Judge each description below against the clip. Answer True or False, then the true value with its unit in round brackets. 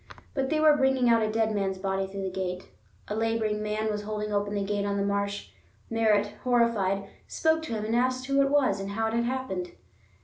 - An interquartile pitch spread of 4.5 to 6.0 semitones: False (3.3 semitones)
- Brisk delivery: True (225 wpm)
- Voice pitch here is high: True (215 Hz)